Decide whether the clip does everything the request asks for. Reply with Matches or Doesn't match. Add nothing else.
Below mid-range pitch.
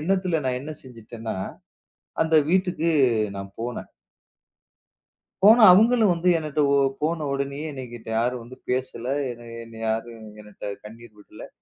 Matches